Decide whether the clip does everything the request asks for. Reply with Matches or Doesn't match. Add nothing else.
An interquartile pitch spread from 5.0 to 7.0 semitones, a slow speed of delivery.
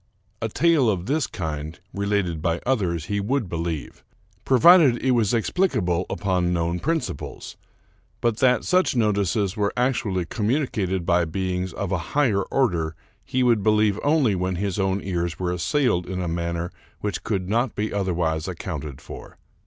Doesn't match